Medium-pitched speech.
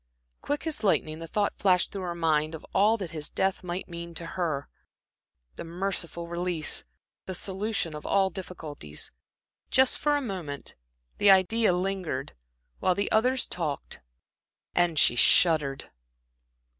Yes: medium, 180 Hz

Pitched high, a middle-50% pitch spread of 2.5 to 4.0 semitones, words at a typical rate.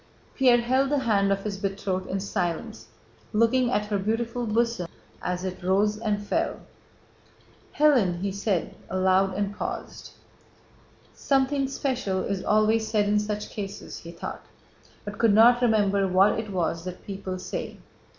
Yes: high, 205 Hz; average, 3.3 semitones; average, 150 wpm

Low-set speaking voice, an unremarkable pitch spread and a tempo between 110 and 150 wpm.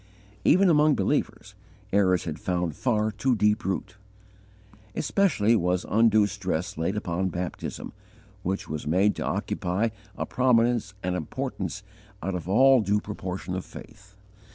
Yes: low, 100 Hz; average, 3.9 semitones; slow, 135 wpm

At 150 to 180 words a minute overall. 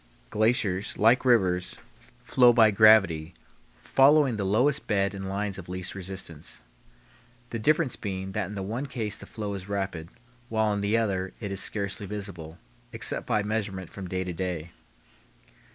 Yes: average, 160 wpm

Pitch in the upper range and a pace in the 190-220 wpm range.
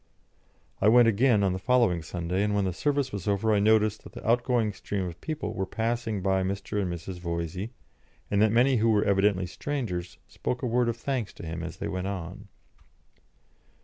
No: low, 105 Hz; average, 200 wpm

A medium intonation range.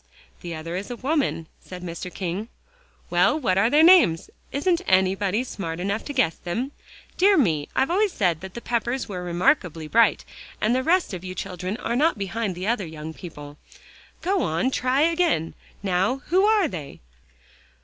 No: wide, 7.6 semitones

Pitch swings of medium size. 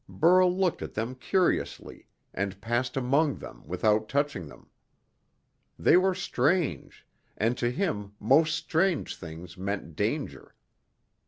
No: wide, 8.7 semitones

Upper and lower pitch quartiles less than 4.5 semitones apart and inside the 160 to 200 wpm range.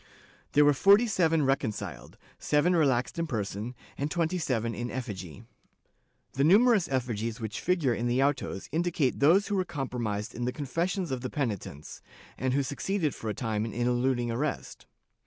No: wide, 5.6 semitones; average, 165 wpm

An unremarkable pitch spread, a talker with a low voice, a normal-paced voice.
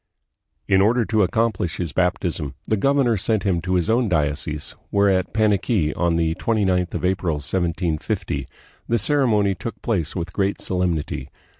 Yes: average, 4.4 semitones; very low, 95 Hz; average, 155 wpm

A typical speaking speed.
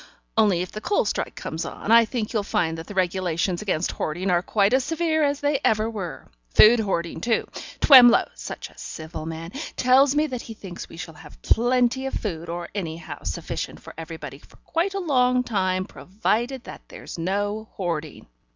Yes: average, 190 wpm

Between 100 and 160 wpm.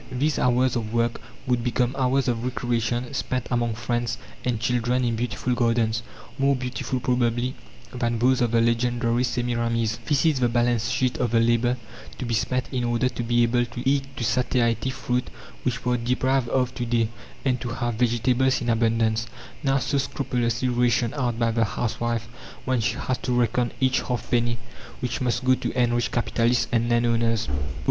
No: average, 180 wpm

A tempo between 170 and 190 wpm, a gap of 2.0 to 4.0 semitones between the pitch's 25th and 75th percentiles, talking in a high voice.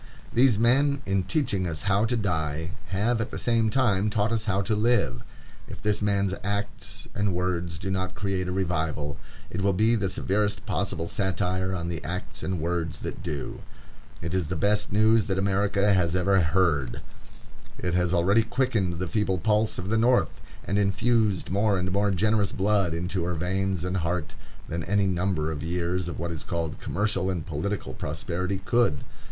No: average, 180 wpm; average, 3.1 semitones; very low, 95 Hz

